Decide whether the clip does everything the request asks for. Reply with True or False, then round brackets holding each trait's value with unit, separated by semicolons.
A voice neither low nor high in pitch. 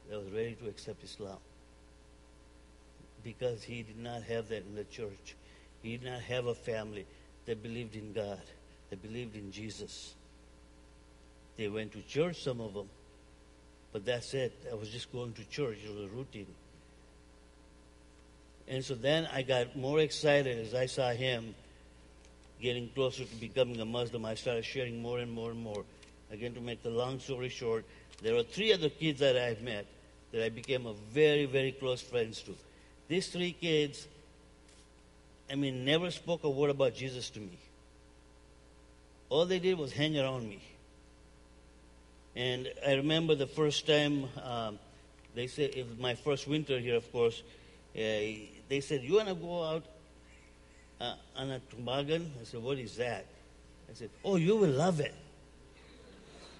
False (115 Hz)